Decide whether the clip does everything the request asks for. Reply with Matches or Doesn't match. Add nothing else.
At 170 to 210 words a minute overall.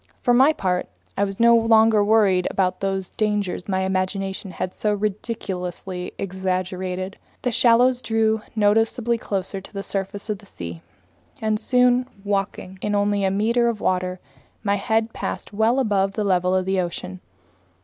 Doesn't match